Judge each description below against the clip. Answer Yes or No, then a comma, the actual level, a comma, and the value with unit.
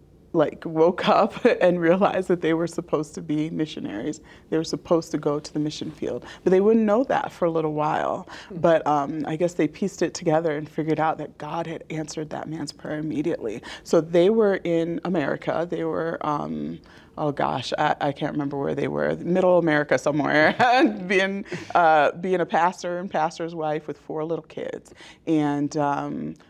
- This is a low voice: No, medium, 160 Hz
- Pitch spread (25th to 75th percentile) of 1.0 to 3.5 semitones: Yes, average, 2.8 semitones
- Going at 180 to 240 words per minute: Yes, average, 190 wpm